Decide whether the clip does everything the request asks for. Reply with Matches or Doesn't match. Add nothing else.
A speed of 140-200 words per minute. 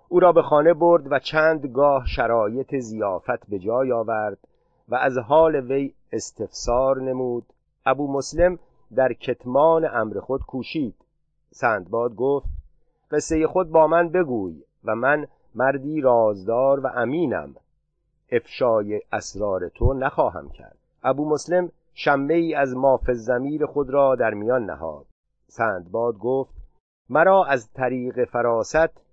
Doesn't match